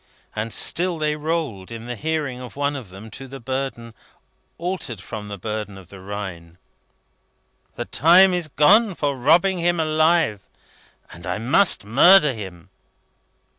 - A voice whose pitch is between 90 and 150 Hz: Yes, low, 135 Hz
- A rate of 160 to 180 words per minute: No, average, 150 wpm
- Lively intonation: Yes, wide, 7.3 semitones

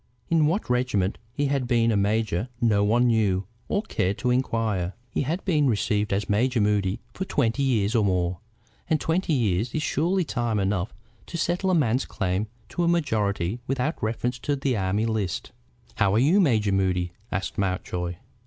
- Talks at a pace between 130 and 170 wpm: No, average, 180 wpm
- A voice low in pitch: Yes, low, 115 Hz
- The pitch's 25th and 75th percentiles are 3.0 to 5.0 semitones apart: No, wide, 5.5 semitones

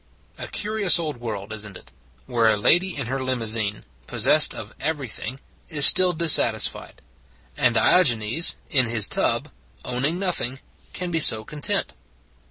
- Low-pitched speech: Yes, low, 130 Hz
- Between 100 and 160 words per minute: Yes, average, 155 wpm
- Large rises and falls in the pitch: Yes, wide, 6.7 semitones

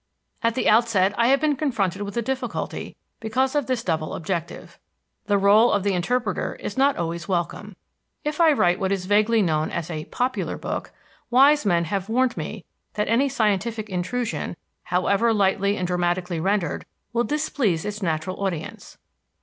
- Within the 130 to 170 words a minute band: Yes, average, 165 wpm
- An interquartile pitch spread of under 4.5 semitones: No, average, 5.0 semitones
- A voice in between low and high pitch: No, high, 205 Hz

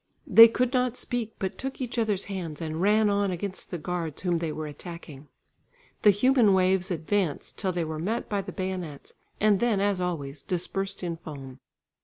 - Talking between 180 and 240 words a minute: Yes, average, 185 wpm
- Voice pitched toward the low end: No, medium, 185 Hz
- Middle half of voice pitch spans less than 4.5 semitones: Yes, average, 4.1 semitones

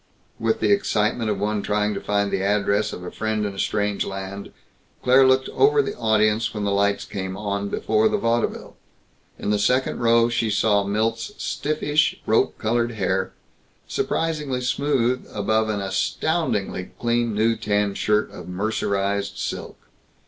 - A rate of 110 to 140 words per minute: No, average, 155 wpm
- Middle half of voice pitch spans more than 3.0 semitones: No, average, 2.7 semitones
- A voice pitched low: Yes, low, 110 Hz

